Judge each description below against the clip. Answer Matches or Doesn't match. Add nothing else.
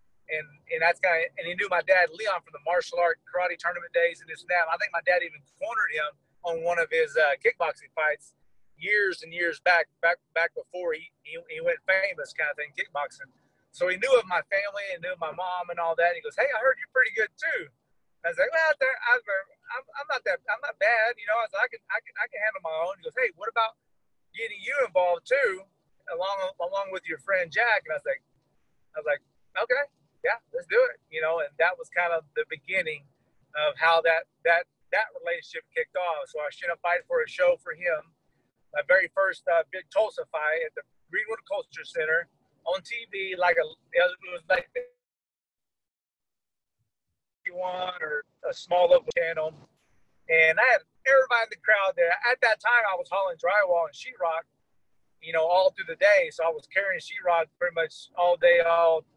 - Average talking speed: Doesn't match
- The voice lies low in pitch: Doesn't match